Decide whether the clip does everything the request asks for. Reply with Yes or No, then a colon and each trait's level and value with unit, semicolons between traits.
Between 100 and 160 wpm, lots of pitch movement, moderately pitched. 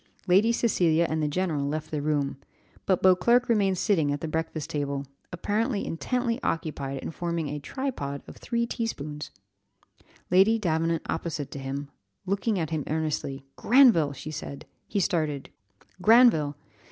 Yes: average, 150 wpm; wide, 5.7 semitones; medium, 165 Hz